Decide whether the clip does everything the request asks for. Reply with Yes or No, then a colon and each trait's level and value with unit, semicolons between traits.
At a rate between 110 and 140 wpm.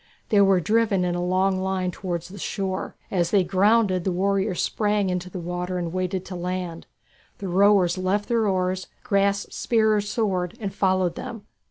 No: average, 180 wpm